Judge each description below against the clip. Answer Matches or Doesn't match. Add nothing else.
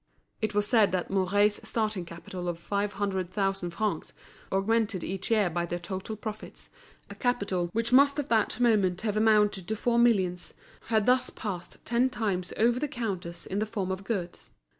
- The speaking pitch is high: Matches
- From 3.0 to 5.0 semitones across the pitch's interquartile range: Matches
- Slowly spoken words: Doesn't match